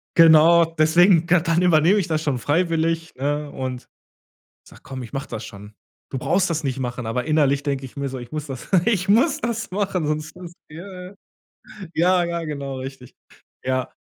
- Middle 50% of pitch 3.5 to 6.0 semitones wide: Yes, average, 4.6 semitones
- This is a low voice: No, medium, 155 Hz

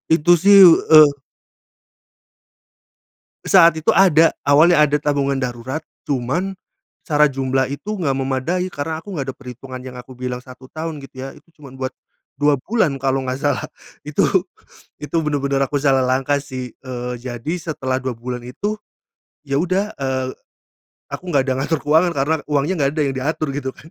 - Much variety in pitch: No, average, 3.3 semitones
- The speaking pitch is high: No, medium, 140 Hz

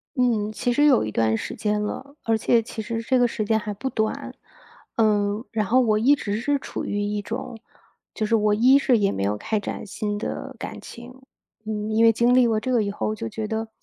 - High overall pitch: Yes, high, 220 Hz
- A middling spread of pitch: No, narrow, 2.3 semitones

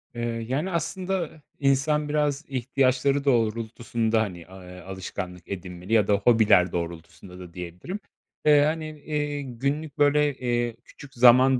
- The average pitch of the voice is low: Yes, low, 125 Hz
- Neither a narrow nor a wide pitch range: No, wide, 7.1 semitones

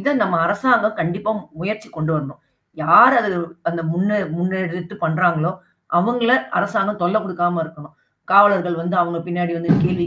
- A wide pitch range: No, average, 3.2 semitones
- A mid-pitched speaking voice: Yes, medium, 180 Hz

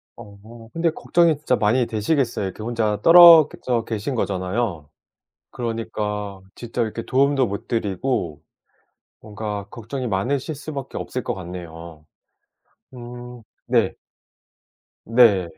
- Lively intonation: No, average, 4.0 semitones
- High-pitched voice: No, low, 115 Hz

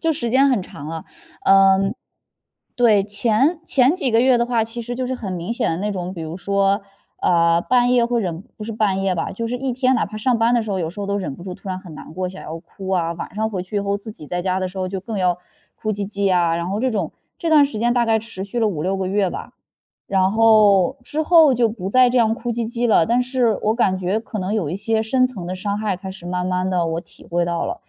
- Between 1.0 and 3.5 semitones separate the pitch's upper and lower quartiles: No, average, 4.4 semitones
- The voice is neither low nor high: No, high, 205 Hz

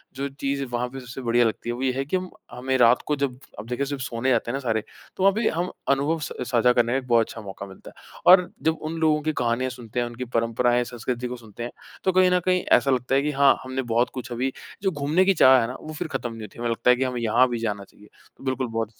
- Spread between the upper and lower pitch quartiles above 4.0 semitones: No, average, 2.9 semitones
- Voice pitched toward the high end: No, low, 125 Hz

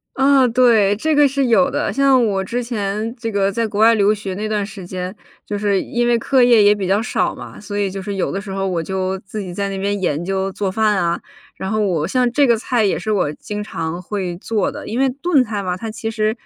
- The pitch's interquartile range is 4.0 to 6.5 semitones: No, average, 3.2 semitones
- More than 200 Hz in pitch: Yes, high, 210 Hz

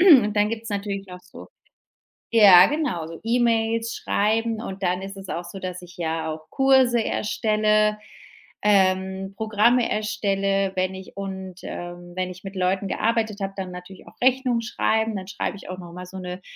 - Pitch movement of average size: Yes, average, 3.2 semitones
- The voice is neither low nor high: No, high, 195 Hz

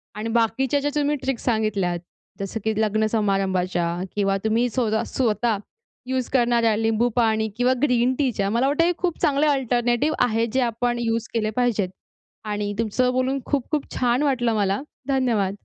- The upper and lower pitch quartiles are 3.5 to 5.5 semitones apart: No, average, 3.1 semitones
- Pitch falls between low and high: No, high, 235 Hz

